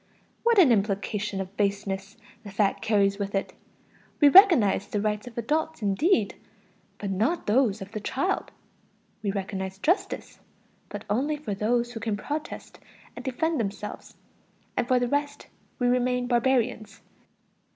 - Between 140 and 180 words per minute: Yes, average, 145 wpm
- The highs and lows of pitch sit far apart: No, average, 4.7 semitones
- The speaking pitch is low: No, high, 220 Hz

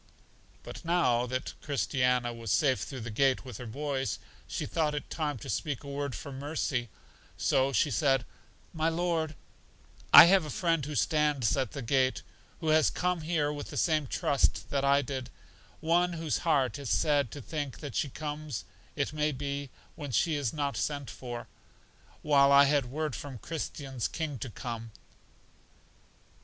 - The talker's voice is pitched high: No, medium, 140 Hz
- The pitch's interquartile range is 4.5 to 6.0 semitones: No, average, 3.0 semitones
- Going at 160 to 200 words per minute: Yes, average, 170 wpm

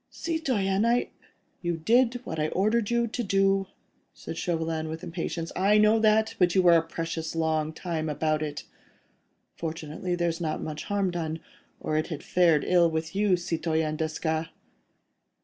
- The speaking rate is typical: Yes, average, 165 wpm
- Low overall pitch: No, medium, 170 Hz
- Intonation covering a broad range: No, average, 3.7 semitones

